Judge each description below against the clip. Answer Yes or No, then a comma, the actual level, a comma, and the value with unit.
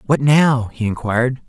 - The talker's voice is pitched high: No, low, 125 Hz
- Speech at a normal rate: Yes, average, 160 wpm